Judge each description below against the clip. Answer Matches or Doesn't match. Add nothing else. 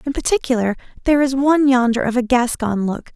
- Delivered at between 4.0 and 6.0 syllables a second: Doesn't match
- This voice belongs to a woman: Matches